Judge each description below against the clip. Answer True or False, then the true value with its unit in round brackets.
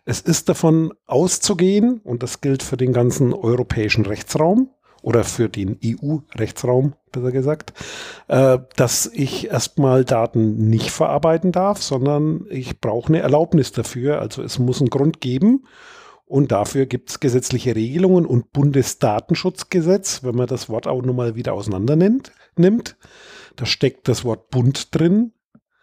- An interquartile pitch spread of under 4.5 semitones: False (5.0 semitones)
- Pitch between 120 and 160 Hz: True (135 Hz)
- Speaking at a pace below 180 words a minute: True (140 wpm)